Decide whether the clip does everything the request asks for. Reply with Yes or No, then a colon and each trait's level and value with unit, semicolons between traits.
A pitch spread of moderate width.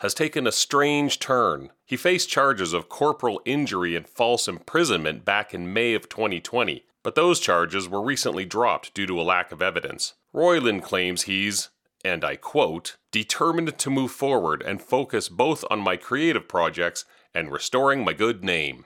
No: wide, 7.5 semitones